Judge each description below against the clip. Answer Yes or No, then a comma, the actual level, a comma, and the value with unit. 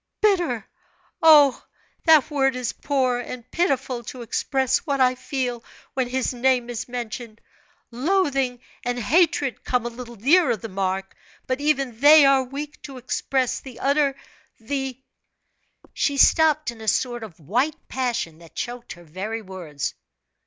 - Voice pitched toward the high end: Yes, very high, 255 Hz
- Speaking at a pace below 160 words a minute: Yes, average, 150 wpm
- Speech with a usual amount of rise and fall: Yes, average, 3.0 semitones